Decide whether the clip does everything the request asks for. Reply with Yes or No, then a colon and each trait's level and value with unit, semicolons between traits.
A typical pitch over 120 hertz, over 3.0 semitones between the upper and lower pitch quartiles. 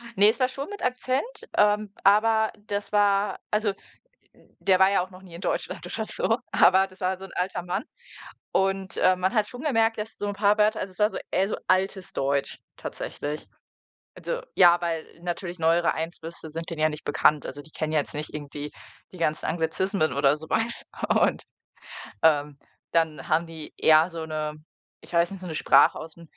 Yes: medium, 185 Hz; average, 4.4 semitones